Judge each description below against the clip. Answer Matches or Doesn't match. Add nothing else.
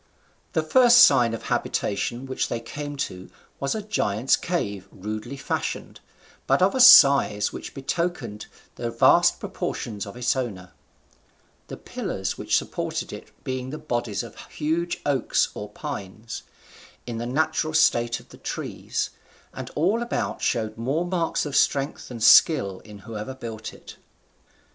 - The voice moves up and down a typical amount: Doesn't match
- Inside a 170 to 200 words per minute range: Doesn't match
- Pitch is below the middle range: Matches